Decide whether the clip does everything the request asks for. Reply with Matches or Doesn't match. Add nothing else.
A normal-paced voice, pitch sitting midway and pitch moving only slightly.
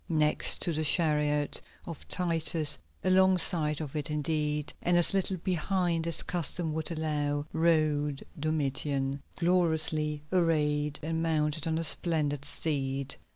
Doesn't match